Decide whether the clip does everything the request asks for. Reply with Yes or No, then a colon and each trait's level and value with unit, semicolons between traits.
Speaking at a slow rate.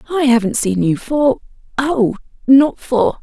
Yes: slow, 130 wpm